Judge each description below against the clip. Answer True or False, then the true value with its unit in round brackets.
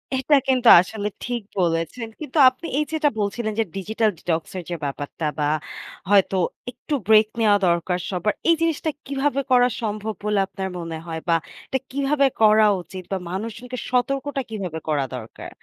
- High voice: True (215 Hz)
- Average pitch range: False (5.8 semitones)